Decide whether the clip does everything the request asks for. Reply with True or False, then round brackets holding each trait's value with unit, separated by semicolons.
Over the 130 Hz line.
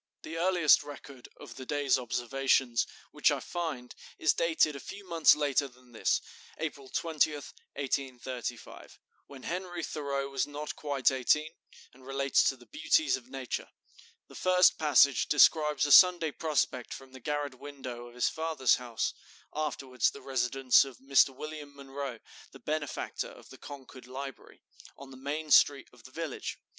True (140 Hz)